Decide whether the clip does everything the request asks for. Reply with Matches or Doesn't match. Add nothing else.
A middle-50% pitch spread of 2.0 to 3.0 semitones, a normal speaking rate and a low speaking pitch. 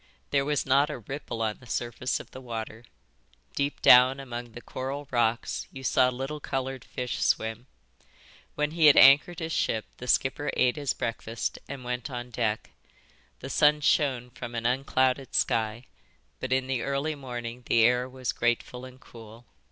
Matches